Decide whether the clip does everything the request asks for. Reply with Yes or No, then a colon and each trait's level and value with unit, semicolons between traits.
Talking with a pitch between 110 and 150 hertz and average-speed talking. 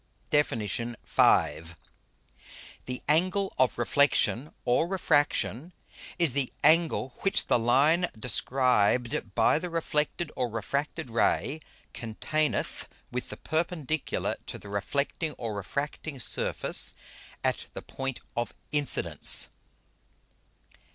No: medium, 140 Hz; slow, 105 wpm